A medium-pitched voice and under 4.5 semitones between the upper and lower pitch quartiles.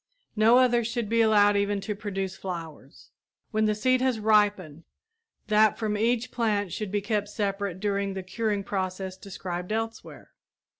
No: high, 205 Hz; narrow, 2.4 semitones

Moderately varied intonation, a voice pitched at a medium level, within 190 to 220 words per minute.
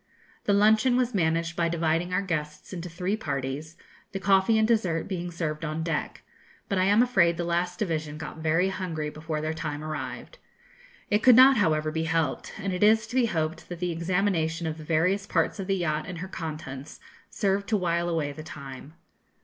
Yes: average, 3.8 semitones; medium, 170 Hz; average, 200 wpm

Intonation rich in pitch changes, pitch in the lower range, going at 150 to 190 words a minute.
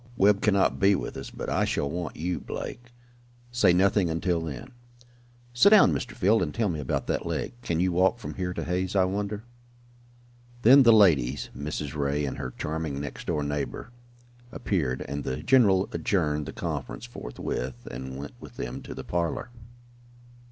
Yes: wide, 5.9 semitones; very low, 90 Hz; average, 175 wpm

